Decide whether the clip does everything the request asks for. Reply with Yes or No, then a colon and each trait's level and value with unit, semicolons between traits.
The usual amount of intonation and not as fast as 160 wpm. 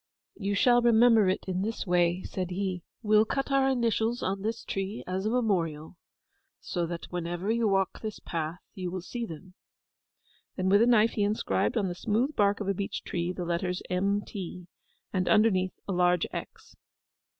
No: average, 3.5 semitones; average, 180 wpm